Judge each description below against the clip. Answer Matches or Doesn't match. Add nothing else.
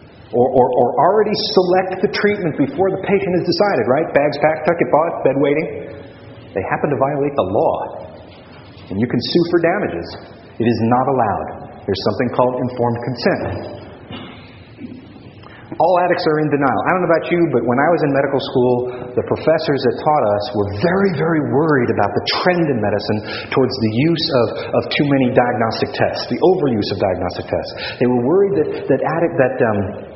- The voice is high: Doesn't match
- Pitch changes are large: Matches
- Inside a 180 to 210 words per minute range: Matches